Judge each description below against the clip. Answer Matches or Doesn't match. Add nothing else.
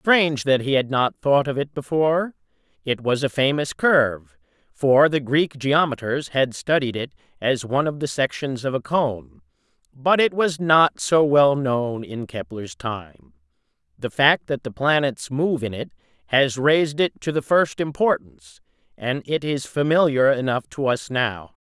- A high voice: Doesn't match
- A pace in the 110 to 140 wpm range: Doesn't match